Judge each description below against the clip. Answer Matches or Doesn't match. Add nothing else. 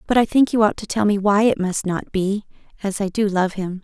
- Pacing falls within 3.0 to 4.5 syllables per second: Doesn't match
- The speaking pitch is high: Matches